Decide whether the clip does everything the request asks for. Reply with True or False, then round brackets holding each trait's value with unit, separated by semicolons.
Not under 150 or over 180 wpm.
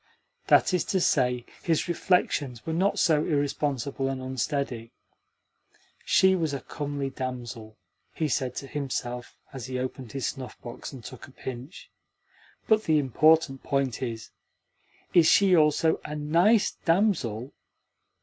False (140 wpm)